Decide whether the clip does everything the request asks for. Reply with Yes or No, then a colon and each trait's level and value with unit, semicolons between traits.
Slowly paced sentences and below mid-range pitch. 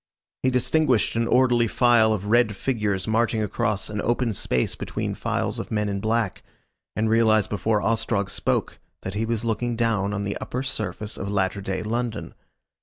No: average, 175 wpm; low, 110 Hz